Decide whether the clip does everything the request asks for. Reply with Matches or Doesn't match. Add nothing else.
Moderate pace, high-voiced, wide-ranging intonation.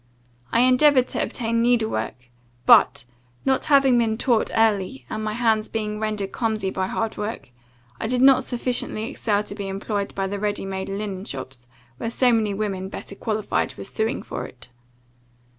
Doesn't match